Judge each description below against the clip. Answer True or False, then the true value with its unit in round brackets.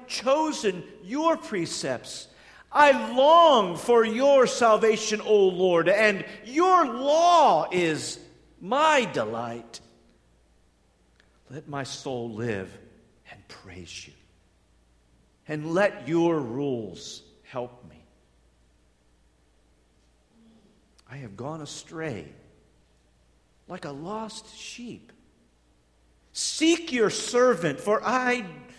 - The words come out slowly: True (90 wpm)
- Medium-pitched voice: True (155 Hz)